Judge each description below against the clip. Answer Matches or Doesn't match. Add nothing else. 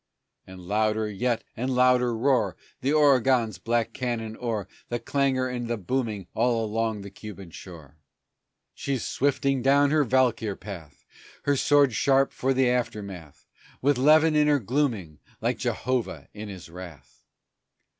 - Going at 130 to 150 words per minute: Matches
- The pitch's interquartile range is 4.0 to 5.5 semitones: Matches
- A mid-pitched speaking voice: Doesn't match